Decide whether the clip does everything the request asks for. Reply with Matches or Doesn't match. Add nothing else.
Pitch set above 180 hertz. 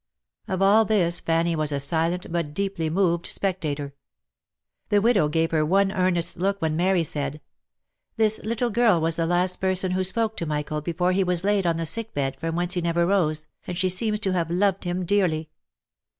Doesn't match